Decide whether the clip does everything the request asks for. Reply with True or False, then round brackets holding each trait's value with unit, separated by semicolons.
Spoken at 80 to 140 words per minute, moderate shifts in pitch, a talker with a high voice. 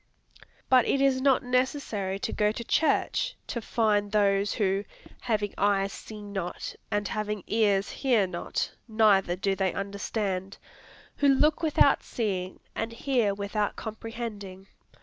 True (135 wpm; 3.1 semitones; 210 Hz)